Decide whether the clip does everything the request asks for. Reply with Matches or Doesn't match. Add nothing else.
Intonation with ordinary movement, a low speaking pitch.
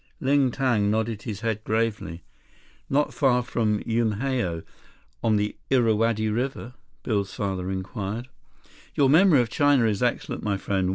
Matches